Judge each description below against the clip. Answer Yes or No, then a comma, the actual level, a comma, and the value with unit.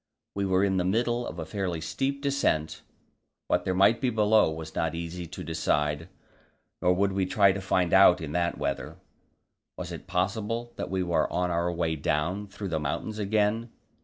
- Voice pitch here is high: No, very low, 95 Hz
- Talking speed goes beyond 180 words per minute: Yes, average, 190 wpm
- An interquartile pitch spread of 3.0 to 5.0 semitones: Yes, average, 3.7 semitones